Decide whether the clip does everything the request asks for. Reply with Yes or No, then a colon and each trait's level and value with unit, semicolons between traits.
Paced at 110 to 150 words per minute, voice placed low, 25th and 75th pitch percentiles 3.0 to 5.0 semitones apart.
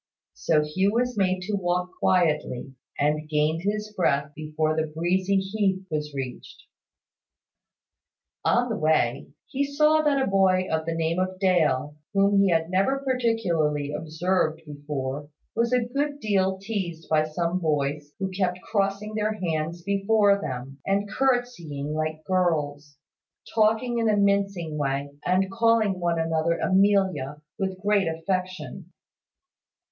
No: average, 140 wpm; medium, 185 Hz; average, 4.6 semitones